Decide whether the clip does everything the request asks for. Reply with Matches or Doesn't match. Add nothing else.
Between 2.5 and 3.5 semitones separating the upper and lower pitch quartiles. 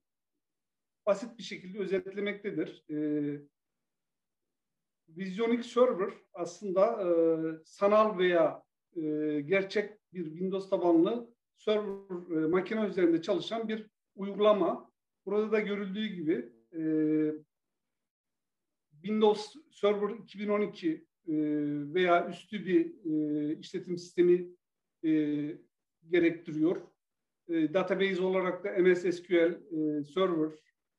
Doesn't match